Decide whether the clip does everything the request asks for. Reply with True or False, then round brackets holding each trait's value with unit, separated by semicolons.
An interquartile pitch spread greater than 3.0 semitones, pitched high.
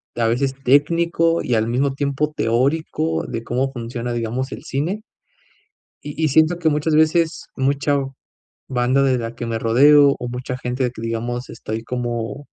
False (3.7 semitones; 130 Hz)